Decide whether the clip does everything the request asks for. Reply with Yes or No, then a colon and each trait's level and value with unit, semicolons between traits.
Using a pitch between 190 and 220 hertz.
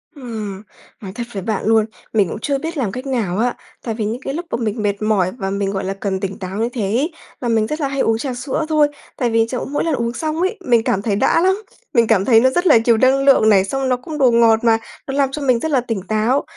No: high, 235 Hz